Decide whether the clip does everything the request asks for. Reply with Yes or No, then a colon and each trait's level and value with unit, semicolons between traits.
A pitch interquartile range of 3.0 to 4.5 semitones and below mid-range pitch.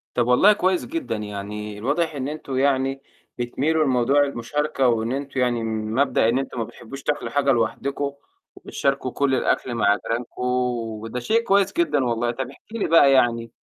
Yes: average, 3.4 semitones; low, 130 Hz